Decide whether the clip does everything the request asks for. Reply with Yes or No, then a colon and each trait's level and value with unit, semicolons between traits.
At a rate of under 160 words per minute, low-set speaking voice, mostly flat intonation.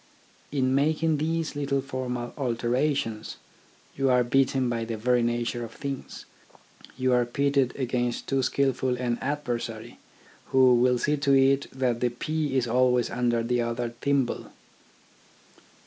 Yes: average, 140 wpm; low, 130 Hz; narrow, 2.3 semitones